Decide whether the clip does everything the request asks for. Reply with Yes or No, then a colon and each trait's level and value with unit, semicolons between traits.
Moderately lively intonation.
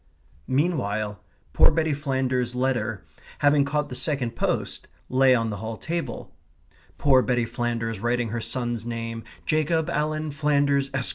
Yes: average, 3.9 semitones